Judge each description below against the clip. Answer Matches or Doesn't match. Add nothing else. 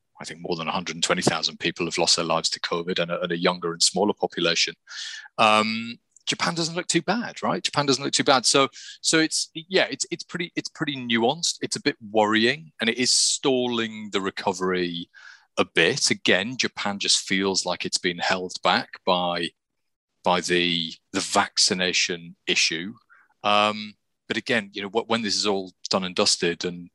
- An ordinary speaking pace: Matches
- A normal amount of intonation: Doesn't match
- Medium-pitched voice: Doesn't match